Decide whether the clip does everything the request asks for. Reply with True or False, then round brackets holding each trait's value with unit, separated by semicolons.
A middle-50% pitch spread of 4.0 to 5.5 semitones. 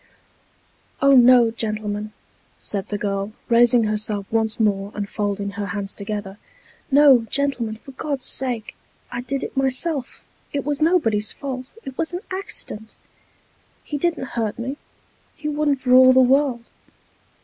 True (4.5 semitones)